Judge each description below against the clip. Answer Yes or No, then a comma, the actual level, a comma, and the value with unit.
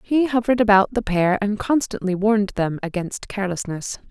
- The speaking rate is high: No, average, 160 wpm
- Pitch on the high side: Yes, high, 205 Hz